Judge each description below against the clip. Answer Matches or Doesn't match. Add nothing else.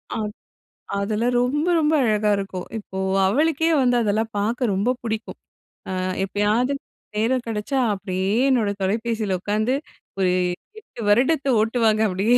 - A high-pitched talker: Matches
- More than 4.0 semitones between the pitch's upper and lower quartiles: Doesn't match